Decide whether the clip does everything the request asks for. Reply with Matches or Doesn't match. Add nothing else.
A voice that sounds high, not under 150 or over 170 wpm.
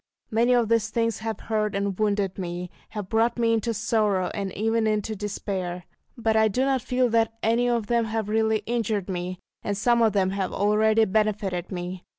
Doesn't match